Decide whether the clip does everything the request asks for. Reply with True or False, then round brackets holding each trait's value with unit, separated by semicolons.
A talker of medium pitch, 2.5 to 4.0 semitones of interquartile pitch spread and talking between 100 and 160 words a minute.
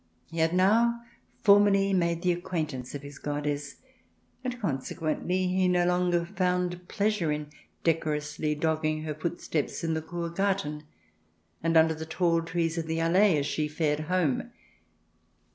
True (165 Hz; 2.9 semitones; 150 wpm)